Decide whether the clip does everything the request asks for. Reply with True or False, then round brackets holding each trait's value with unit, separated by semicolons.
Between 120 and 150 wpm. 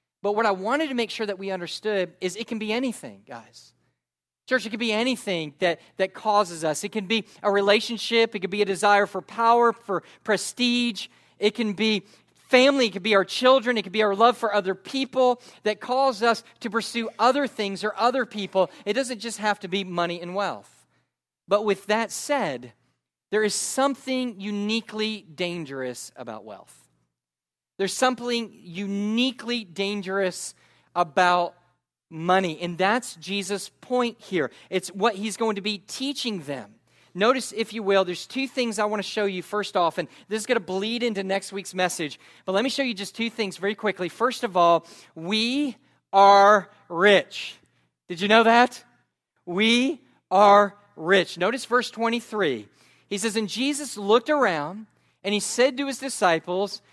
False (175 wpm)